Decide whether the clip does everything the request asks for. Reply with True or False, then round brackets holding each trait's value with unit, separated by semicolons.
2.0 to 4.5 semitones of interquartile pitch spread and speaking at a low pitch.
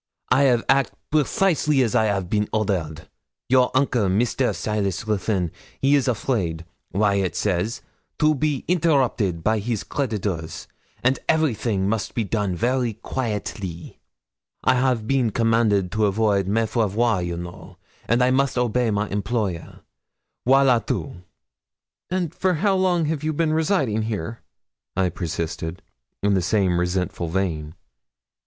False (5.4 semitones; 110 Hz)